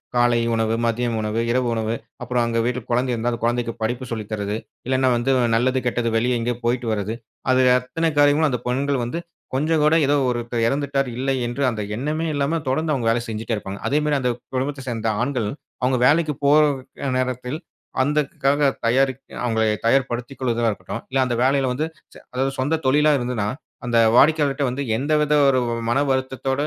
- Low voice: Yes, low, 125 Hz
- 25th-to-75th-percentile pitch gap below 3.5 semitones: Yes, average, 3.0 semitones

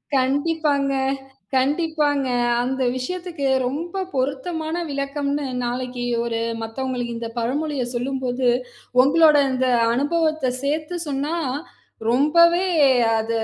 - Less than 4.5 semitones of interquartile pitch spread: Yes, average, 3.6 semitones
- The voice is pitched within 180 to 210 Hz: No, very high, 280 Hz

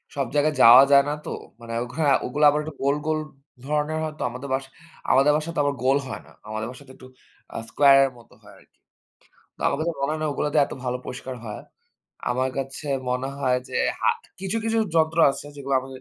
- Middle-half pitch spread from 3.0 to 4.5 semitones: No, narrow, 2.6 semitones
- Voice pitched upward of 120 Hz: Yes, medium, 140 Hz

